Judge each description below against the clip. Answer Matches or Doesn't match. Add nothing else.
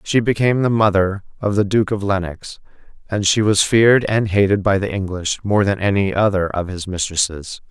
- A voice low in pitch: Matches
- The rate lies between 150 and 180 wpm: Doesn't match